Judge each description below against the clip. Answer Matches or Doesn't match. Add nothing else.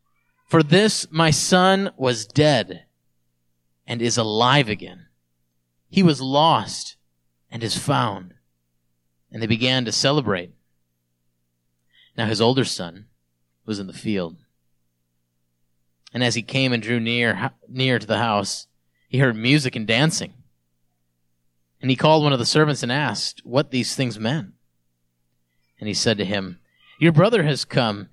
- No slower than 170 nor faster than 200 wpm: Doesn't match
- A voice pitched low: Matches